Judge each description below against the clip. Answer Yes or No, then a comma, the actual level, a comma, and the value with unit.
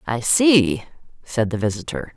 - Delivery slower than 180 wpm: Yes, average, 140 wpm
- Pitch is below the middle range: Yes, low, 130 Hz